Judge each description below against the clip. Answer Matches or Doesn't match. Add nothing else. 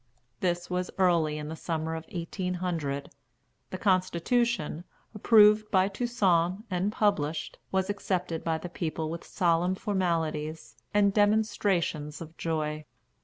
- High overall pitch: Doesn't match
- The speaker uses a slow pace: Matches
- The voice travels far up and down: Doesn't match